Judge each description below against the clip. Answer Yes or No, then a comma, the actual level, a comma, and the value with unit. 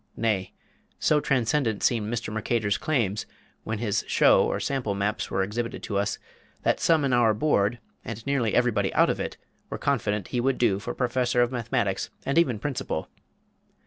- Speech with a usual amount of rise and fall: Yes, average, 3.3 semitones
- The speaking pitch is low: Yes, low, 115 Hz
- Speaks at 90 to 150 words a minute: No, average, 175 wpm